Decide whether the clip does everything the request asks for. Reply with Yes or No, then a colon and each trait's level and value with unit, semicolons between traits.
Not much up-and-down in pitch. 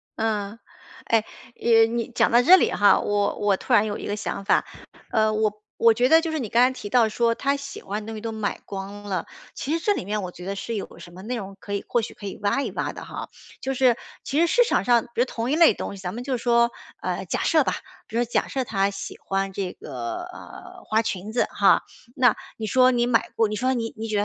No: average, 3.4 semitones